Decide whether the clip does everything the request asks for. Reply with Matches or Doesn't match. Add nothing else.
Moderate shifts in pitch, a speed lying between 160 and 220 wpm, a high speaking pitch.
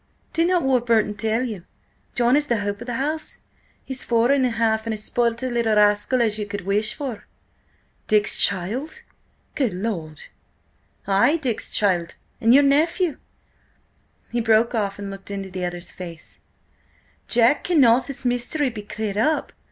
Matches